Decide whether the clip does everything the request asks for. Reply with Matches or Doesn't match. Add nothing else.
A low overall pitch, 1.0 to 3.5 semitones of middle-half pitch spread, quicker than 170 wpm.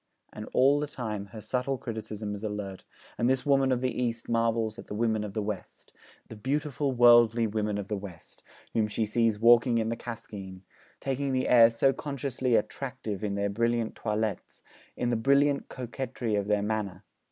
Matches